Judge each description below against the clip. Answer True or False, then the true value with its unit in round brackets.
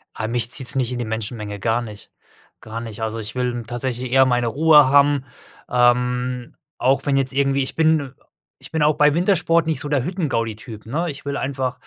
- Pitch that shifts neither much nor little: True (3.4 semitones)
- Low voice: True (125 Hz)